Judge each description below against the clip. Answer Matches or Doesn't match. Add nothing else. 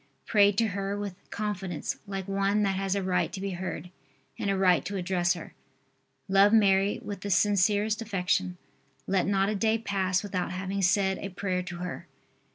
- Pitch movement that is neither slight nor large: Doesn't match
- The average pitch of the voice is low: Doesn't match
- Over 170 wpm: Matches